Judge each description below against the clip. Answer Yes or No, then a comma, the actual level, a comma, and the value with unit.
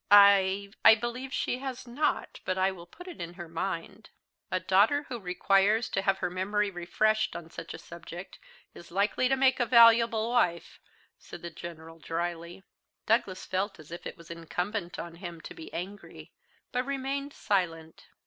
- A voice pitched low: No, high, 195 Hz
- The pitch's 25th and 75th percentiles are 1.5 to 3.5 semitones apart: No, average, 5.1 semitones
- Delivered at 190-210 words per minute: No, average, 170 wpm